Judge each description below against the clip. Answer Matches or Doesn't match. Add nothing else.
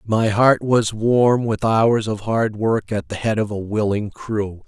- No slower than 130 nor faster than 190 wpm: Doesn't match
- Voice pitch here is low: Matches